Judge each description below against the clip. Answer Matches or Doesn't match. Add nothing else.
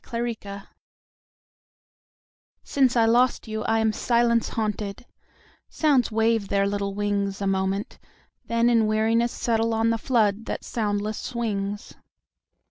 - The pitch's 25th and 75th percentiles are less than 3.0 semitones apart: Matches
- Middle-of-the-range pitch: Doesn't match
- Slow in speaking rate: Matches